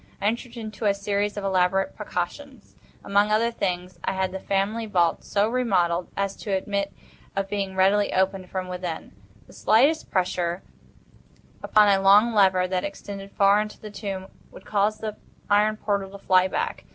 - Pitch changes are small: Yes, narrow, 2.0 semitones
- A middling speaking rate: Yes, average, 170 wpm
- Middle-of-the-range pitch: No, high, 200 Hz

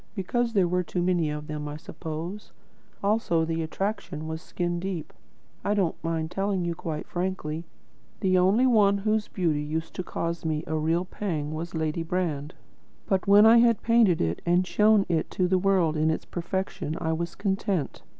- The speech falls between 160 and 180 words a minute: Yes, average, 175 wpm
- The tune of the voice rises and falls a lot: No, average, 3.6 semitones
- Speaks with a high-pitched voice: No, medium, 175 Hz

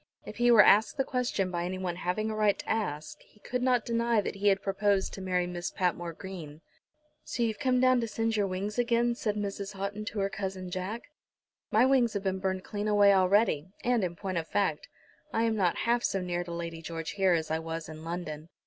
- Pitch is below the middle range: No, high, 195 Hz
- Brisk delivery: Yes, fast, 225 wpm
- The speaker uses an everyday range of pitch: Yes, average, 3.9 semitones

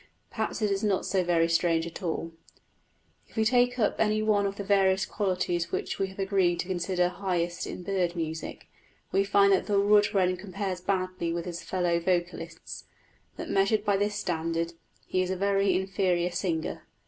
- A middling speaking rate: Yes, average, 180 wpm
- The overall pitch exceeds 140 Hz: Yes, high, 190 Hz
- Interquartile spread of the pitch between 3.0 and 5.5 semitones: No, narrow, 2.4 semitones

